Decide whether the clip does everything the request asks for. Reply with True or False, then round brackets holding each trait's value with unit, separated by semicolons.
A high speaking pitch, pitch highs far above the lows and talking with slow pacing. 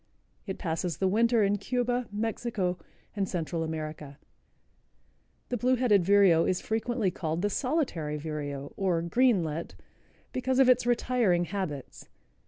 True (195 Hz; 6.6 semitones; 130 wpm)